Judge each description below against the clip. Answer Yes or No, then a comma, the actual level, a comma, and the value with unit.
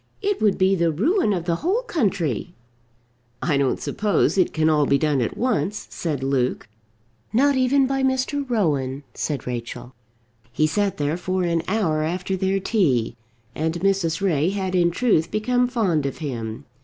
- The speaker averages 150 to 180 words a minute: Yes, average, 170 wpm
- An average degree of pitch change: No, wide, 6.1 semitones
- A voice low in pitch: No, medium, 180 Hz